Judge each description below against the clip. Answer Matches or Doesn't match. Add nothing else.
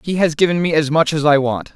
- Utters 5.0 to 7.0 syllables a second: Matches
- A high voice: Doesn't match